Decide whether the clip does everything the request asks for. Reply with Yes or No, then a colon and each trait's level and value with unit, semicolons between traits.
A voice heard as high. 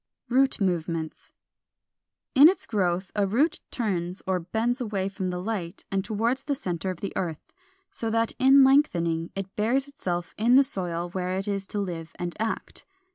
Yes: high, 195 Hz